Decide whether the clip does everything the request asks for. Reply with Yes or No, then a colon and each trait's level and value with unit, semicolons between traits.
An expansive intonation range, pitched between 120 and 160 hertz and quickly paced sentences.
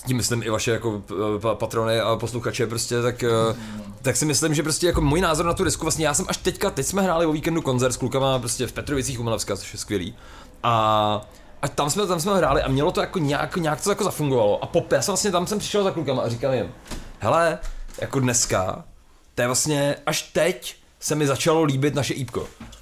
Yes: wide, 5.8 semitones; low, 135 Hz; fast, 220 wpm